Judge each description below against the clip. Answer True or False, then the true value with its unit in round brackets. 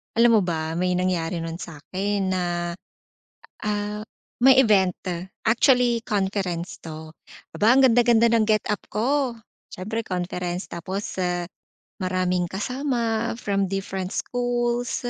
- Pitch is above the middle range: True (200 Hz)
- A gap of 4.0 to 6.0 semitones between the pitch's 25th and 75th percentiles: True (4.3 semitones)